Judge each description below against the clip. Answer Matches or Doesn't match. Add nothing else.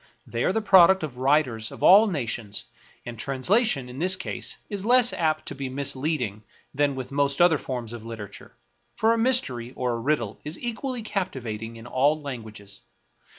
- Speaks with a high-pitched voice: Doesn't match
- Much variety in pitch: Matches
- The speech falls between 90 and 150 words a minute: Doesn't match